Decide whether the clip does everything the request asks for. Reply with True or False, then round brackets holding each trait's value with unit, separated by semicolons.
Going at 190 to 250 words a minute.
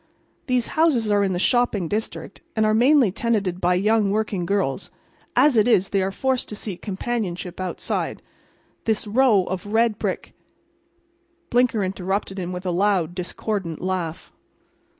False (150 wpm)